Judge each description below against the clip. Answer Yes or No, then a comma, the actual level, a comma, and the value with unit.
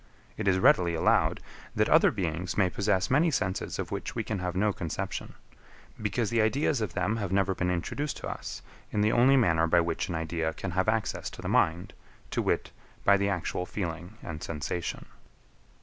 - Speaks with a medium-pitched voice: No, very low, 95 Hz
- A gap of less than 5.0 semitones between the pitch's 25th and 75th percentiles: Yes, average, 3.8 semitones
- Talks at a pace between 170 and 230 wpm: Yes, average, 195 wpm